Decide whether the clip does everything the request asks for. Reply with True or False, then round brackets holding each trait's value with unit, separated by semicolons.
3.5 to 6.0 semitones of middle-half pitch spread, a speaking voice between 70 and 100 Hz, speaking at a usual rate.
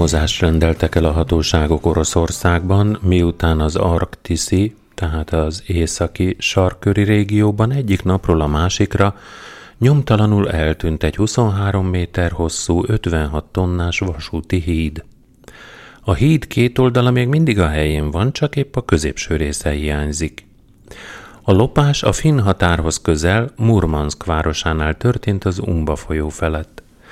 True (4.5 semitones; 90 Hz; 120 wpm)